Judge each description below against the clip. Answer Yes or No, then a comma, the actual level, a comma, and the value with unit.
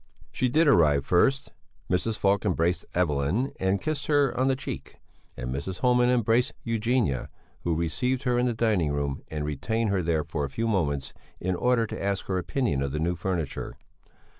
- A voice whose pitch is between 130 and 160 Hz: No, very low, 95 Hz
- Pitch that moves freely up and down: Yes, wide, 7.8 semitones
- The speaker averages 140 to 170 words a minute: No, average, 185 wpm